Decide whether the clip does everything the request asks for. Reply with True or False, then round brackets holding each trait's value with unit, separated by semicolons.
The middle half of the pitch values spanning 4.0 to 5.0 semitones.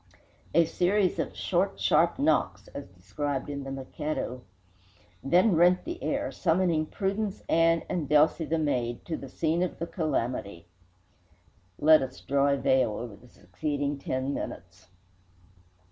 True (4.6 semitones)